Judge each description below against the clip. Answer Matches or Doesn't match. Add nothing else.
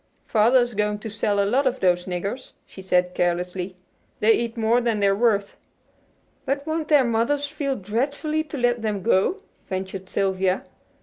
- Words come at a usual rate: Matches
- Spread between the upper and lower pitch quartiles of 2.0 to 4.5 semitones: Doesn't match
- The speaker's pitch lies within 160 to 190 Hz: Doesn't match